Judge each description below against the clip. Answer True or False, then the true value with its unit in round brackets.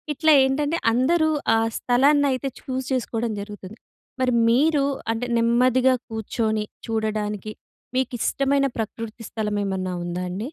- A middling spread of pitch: True (3.6 semitones)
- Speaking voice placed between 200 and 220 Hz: False (235 Hz)